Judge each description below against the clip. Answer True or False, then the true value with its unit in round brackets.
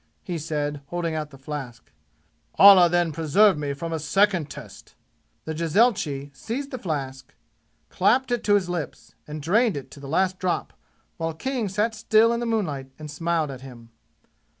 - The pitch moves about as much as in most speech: False (5.8 semitones)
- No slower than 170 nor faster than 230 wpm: True (175 wpm)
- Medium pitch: True (165 Hz)